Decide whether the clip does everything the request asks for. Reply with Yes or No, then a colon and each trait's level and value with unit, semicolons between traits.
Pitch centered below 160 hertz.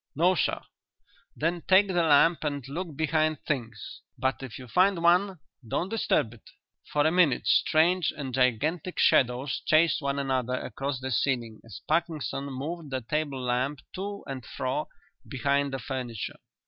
Yes: medium, 140 Hz